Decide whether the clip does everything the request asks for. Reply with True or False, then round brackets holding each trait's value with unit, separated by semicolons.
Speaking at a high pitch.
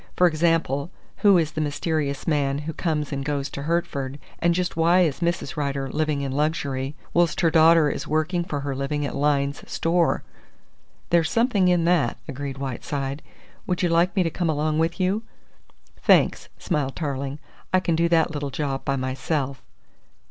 False (155 Hz)